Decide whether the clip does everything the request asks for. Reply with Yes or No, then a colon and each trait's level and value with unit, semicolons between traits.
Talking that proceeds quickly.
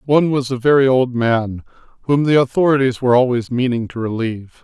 No: average, 180 wpm